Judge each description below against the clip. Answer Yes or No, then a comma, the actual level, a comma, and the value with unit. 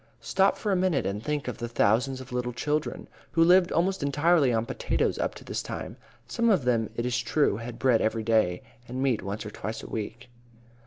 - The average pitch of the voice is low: Yes, low, 125 Hz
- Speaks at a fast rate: Yes, fast, 215 wpm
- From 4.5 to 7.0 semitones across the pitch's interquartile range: Yes, average, 5.1 semitones